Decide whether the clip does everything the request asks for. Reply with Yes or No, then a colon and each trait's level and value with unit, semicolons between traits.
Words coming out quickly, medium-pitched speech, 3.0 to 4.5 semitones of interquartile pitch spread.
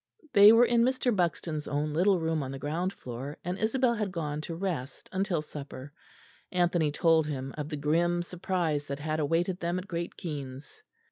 No: average, 185 wpm; medium, 165 Hz; average, 3.8 semitones